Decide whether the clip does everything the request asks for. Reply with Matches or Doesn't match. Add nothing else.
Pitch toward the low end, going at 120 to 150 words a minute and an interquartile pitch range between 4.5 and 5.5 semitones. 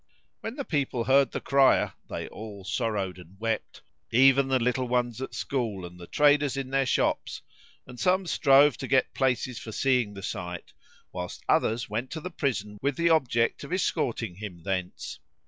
Doesn't match